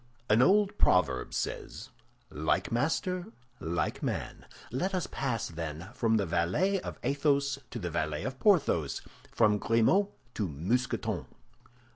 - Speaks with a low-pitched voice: Yes, low, 115 Hz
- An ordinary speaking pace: No, slow, 130 wpm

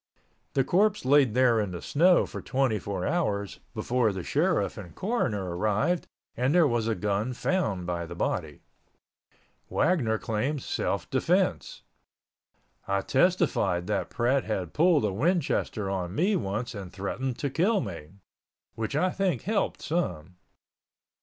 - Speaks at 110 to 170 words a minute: Yes, average, 140 wpm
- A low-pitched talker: Yes, low, 115 Hz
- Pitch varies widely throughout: Yes, wide, 7.6 semitones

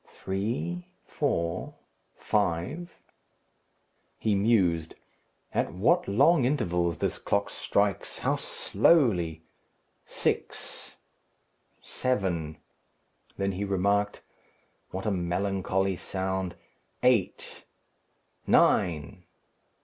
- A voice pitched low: Yes, very low, 95 Hz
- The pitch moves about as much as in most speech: Yes, average, 3.5 semitones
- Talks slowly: Yes, slow, 75 wpm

